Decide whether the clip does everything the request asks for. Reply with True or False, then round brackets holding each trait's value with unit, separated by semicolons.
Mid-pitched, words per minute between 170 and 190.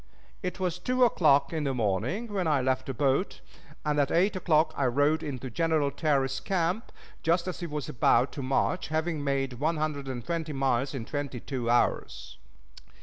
True (145 Hz; 185 wpm)